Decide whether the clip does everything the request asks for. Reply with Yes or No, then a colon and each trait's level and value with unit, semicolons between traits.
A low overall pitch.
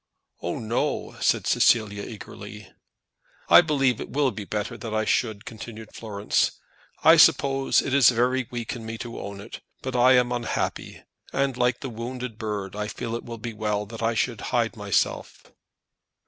Yes: low, 115 Hz